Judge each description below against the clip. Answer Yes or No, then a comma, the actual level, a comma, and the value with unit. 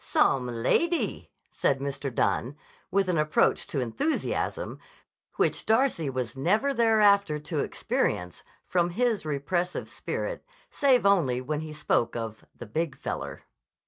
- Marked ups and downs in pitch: Yes, wide, 7.1 semitones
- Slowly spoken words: Yes, slow, 130 wpm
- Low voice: No, medium, 155 Hz